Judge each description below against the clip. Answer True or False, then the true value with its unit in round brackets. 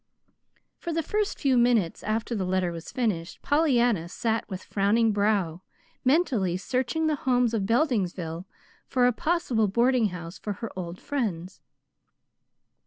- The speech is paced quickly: False (140 wpm)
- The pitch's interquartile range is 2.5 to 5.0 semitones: False (5.4 semitones)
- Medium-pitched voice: False (220 Hz)